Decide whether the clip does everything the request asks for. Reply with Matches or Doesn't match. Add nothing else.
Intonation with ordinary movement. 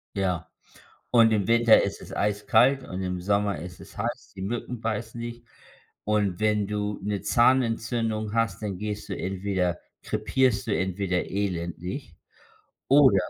Matches